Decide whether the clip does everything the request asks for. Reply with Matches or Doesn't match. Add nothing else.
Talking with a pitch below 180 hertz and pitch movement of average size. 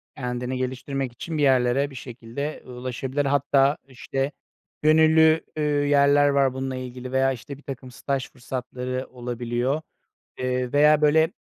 Doesn't match